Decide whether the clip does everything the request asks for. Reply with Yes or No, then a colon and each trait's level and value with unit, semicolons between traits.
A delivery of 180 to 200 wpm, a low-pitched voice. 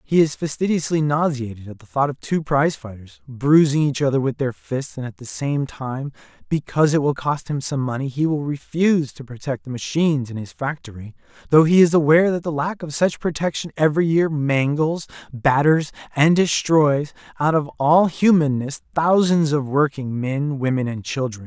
No: average, 185 wpm; medium, 145 Hz